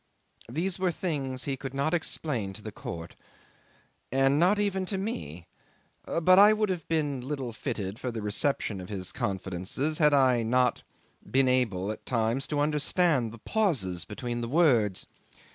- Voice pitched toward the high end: No, low, 130 Hz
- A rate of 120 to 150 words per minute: No, average, 160 wpm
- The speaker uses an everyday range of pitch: No, wide, 6.3 semitones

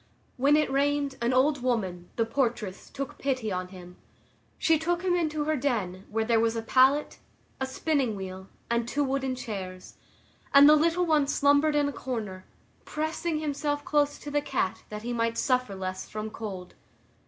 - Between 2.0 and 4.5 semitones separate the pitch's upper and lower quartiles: No, average, 5.3 semitones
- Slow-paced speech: No, average, 175 wpm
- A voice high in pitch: Yes, very high, 260 Hz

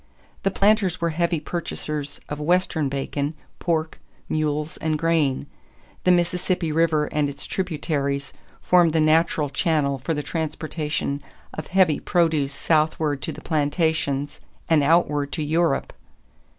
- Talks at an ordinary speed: No, slow, 130 wpm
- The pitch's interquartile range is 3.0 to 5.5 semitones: No, narrow, 2.5 semitones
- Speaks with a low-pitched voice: No, medium, 155 Hz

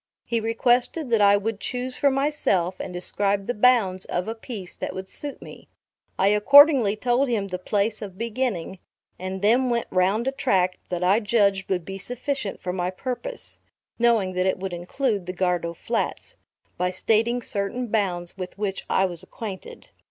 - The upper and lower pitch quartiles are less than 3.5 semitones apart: No, average, 4.4 semitones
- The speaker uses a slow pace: No, average, 175 wpm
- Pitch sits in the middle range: No, high, 205 Hz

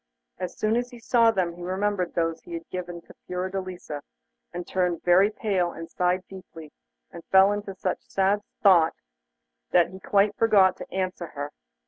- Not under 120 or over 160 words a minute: No, average, 170 wpm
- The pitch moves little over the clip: Yes, narrow, 2.3 semitones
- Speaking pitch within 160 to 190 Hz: Yes, medium, 185 Hz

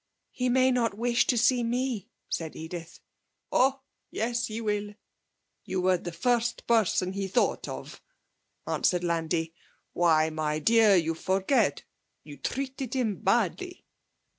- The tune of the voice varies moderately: No, wide, 5.8 semitones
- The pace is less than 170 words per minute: Yes, slow, 135 wpm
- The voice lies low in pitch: No, high, 210 Hz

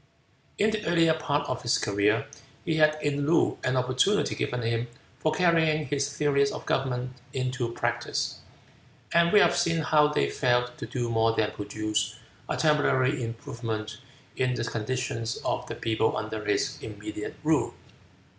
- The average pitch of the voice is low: Yes, low, 130 Hz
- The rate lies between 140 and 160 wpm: Yes, average, 155 wpm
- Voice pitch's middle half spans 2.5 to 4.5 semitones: No, average, 4.9 semitones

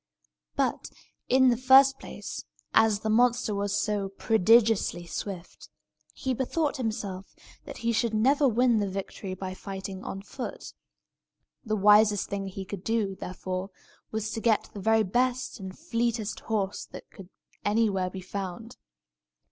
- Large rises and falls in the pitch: No, average, 3.2 semitones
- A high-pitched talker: Yes, high, 215 Hz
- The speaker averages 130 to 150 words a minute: Yes, average, 145 wpm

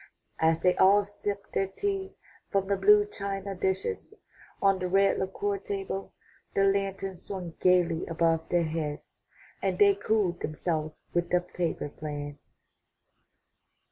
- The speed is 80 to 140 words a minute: Yes, slow, 135 wpm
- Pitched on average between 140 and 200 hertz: Yes, high, 190 Hz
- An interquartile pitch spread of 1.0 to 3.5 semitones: Yes, average, 2.9 semitones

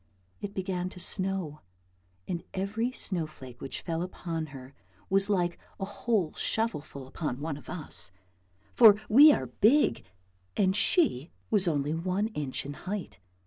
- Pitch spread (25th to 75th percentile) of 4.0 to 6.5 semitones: Yes, average, 5.1 semitones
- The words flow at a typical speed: Yes, average, 150 wpm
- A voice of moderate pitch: Yes, medium, 180 Hz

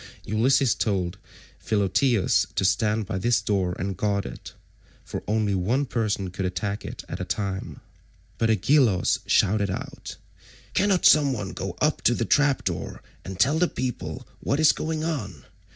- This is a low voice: Yes, low, 105 Hz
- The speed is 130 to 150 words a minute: No, average, 160 wpm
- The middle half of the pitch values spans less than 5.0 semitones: No, wide, 5.5 semitones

